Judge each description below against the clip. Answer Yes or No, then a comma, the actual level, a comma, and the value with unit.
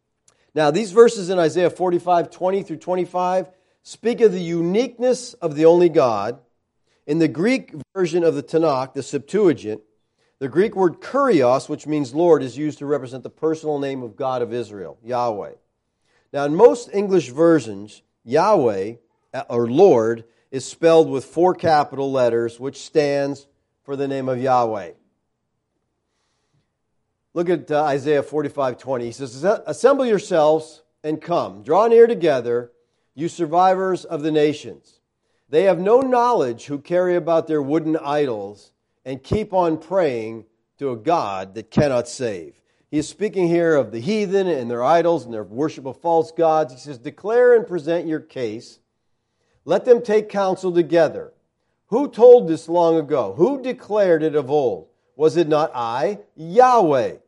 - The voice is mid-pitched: Yes, medium, 155 Hz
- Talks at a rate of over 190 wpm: No, average, 155 wpm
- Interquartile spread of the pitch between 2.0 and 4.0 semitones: No, average, 5.2 semitones